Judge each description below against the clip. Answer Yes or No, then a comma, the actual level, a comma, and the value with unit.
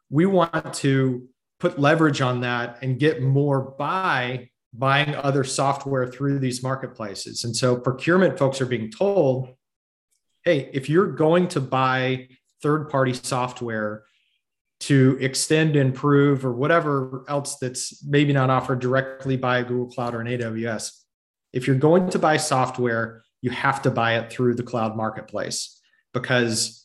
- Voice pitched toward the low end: Yes, low, 130 Hz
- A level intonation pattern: Yes, narrow, 2.3 semitones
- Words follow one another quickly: No, average, 145 wpm